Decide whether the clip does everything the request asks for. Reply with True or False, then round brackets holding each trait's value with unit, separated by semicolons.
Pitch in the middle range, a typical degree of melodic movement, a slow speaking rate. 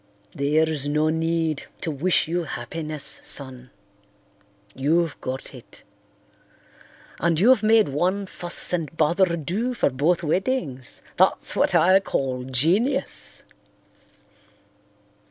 True (160 Hz; 4.1 semitones; 105 wpm)